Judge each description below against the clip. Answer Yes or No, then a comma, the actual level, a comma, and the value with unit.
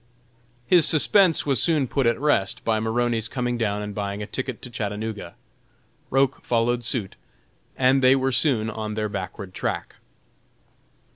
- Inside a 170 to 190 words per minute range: No, average, 150 wpm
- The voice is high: No, low, 115 Hz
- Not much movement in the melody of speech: No, average, 3.8 semitones